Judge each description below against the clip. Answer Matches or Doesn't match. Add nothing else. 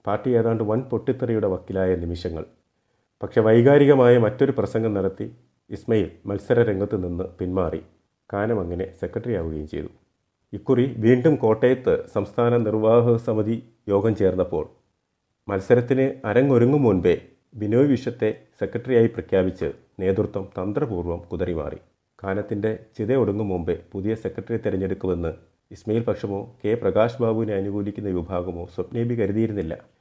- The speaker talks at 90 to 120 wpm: Matches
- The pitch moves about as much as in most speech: Matches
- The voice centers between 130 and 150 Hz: Doesn't match